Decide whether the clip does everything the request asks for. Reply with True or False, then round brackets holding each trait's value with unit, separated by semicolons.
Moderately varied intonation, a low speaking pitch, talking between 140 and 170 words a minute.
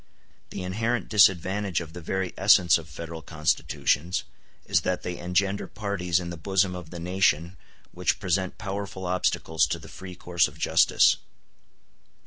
False (2.3 semitones; 90 Hz; 150 wpm)